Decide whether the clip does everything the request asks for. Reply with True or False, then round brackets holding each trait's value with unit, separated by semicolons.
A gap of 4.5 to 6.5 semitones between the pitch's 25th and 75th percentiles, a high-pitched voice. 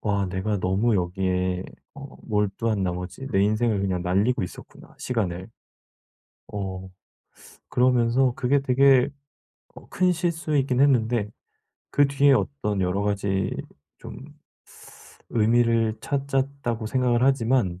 False (5.3 semitones; 115 Hz)